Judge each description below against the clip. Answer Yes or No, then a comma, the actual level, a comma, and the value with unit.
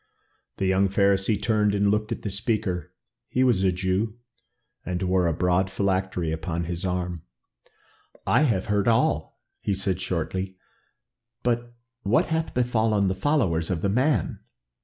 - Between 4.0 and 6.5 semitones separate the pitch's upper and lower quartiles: No, average, 3.1 semitones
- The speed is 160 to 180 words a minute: No, average, 150 wpm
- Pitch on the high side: No, very low, 95 Hz